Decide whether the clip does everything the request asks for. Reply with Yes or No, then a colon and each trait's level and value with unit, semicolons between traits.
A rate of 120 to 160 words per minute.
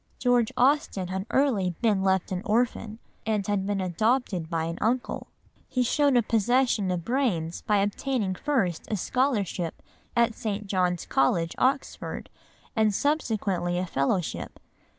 Yes: average, 140 wpm